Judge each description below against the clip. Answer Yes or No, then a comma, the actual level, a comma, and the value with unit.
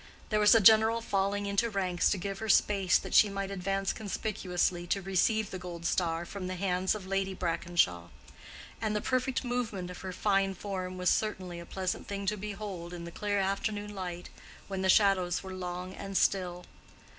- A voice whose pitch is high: Yes, high, 195 Hz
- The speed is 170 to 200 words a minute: Yes, average, 190 wpm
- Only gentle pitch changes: Yes, narrow, 2.2 semitones